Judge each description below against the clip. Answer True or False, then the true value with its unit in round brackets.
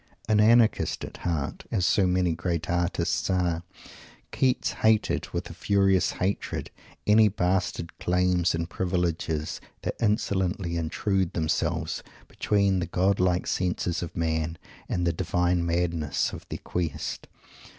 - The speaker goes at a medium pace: False (130 wpm)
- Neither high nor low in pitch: False (90 Hz)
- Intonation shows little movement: True (2.3 semitones)